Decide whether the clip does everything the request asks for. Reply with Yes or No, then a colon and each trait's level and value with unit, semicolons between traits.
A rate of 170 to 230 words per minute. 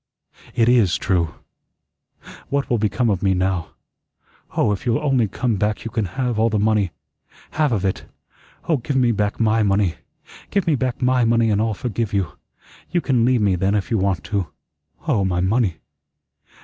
Yes: average, 185 wpm